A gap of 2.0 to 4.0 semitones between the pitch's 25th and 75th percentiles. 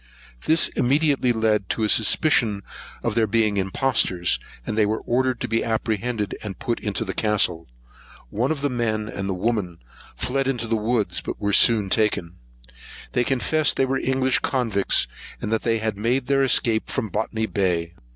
Yes: average, 3.3 semitones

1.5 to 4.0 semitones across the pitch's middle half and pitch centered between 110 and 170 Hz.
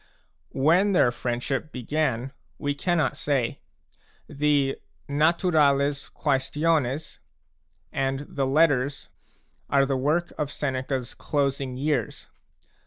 Yes: narrow, 2.4 semitones; medium, 140 Hz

